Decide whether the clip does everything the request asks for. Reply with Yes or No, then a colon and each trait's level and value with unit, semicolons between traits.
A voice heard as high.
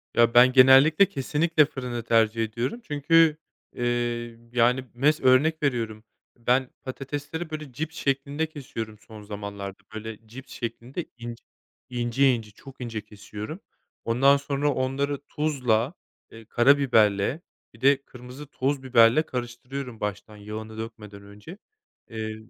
No: low, 125 Hz